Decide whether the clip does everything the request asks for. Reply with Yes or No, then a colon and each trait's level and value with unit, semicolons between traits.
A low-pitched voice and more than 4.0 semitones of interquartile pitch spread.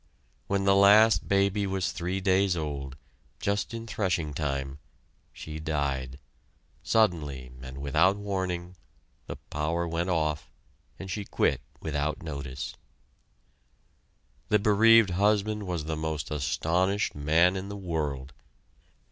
Yes: very low, 85 Hz; average, 4.9 semitones